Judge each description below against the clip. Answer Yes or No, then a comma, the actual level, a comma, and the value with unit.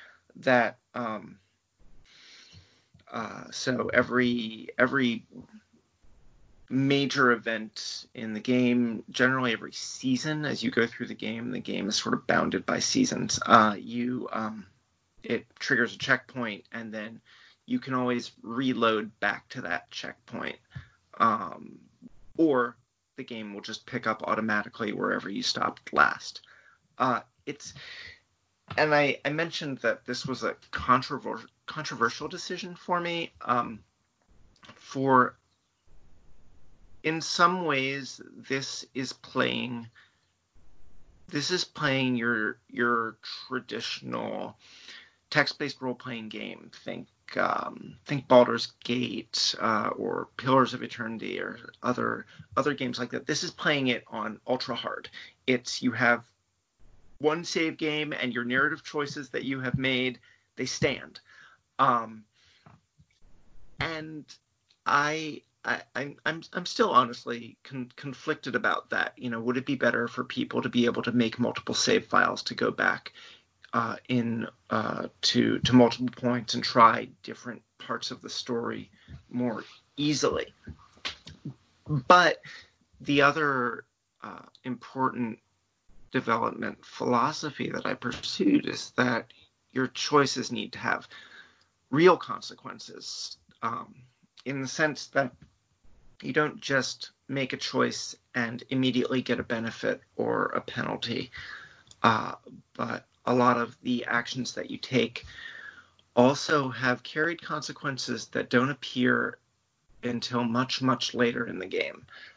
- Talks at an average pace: No, slow, 130 wpm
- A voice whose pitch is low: Yes, low, 125 Hz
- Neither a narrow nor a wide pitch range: Yes, average, 3.1 semitones